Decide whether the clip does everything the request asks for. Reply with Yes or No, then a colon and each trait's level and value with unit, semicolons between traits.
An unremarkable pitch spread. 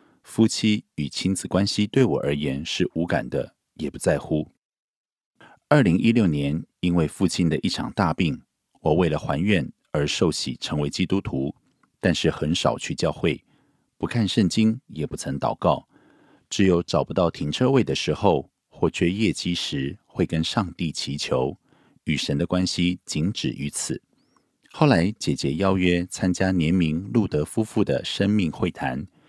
Yes: average, 4.2 semitones